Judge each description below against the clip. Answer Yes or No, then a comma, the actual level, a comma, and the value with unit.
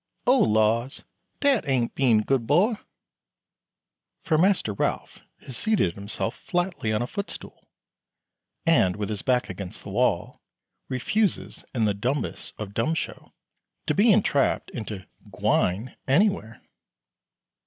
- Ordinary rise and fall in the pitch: No, wide, 8.6 semitones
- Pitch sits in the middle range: No, low, 125 Hz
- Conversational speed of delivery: No, slow, 125 wpm